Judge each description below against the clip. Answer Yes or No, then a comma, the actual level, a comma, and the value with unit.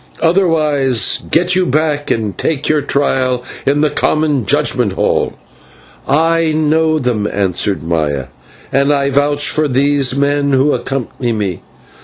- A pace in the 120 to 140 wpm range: Yes, slow, 135 wpm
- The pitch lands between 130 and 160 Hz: Yes, medium, 140 Hz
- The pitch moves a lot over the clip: No, average, 3.7 semitones